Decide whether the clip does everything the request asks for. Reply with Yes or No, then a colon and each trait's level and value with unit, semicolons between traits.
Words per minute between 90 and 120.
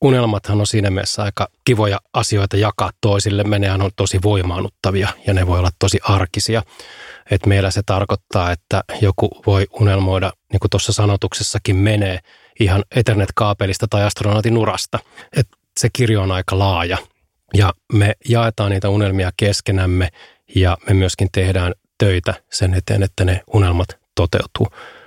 No: average, 145 wpm